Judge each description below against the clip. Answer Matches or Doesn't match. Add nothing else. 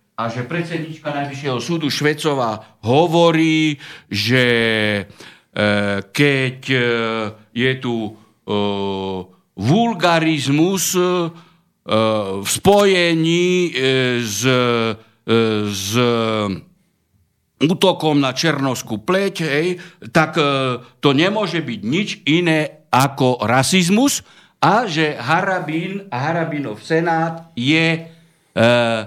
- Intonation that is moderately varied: Doesn't match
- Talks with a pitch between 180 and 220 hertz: Doesn't match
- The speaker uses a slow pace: Matches